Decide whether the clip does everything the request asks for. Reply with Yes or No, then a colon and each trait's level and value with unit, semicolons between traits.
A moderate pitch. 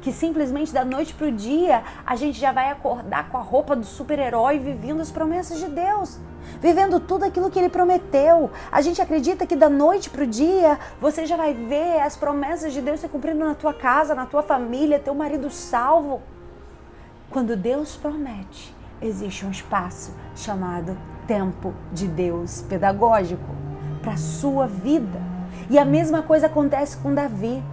No: very high, 285 Hz